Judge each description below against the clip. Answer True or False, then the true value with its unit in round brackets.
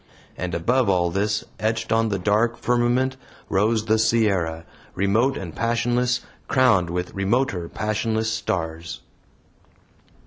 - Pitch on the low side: True (110 Hz)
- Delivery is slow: True (115 wpm)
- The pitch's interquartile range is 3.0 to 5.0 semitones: True (4.3 semitones)